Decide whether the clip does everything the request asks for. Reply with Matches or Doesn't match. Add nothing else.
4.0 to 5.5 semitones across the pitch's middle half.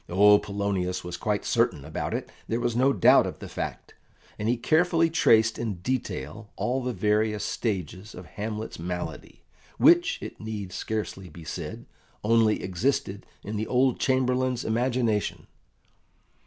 Matches